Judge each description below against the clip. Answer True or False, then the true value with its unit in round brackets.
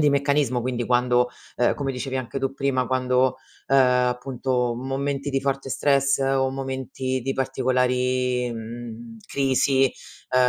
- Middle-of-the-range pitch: False (130 Hz)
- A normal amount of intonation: False (1.5 semitones)